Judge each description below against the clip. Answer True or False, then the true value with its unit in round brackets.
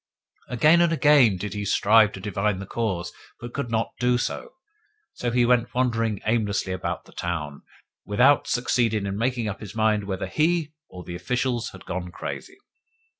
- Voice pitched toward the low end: True (115 Hz)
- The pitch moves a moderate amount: True (4.0 semitones)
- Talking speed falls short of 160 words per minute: False (175 wpm)